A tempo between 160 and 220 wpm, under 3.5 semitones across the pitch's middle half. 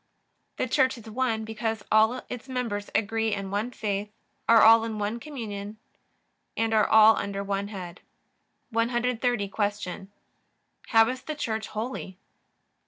No: average, 145 wpm; narrow, 2.5 semitones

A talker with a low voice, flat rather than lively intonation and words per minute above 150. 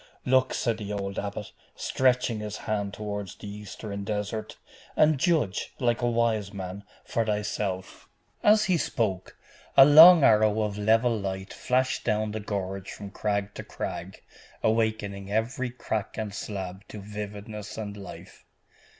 No: low, 105 Hz; narrow, 2.3 semitones; average, 145 wpm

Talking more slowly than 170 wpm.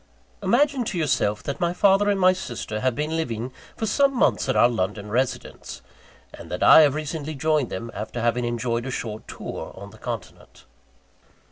No: average, 180 wpm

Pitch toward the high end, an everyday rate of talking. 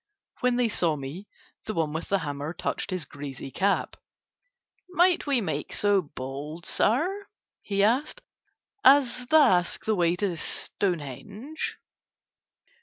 No: high, 195 Hz; slow, 130 wpm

